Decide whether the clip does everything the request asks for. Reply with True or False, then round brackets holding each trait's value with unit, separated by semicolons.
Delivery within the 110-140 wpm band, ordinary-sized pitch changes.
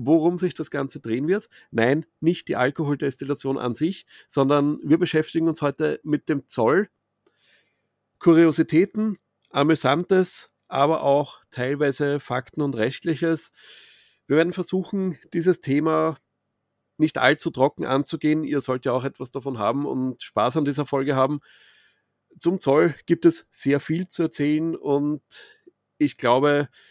True (135 wpm; 3.1 semitones)